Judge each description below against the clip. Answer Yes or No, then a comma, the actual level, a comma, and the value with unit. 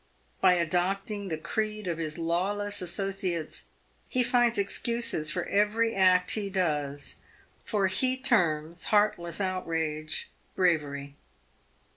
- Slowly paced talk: Yes, slow, 115 wpm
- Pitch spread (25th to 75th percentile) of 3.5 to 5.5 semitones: Yes, average, 3.9 semitones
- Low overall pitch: No, medium, 185 Hz